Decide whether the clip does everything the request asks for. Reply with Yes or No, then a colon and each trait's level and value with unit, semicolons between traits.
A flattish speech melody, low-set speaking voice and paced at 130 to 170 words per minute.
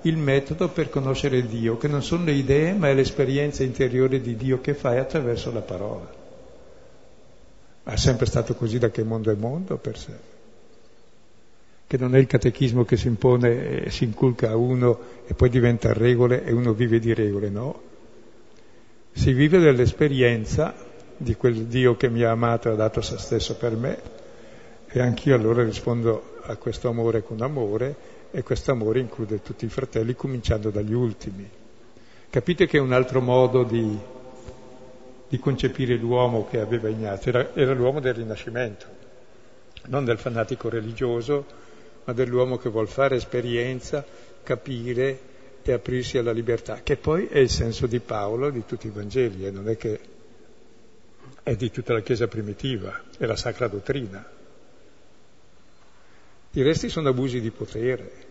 Yes: narrow, 2.3 semitones; low, 125 Hz; average, 160 wpm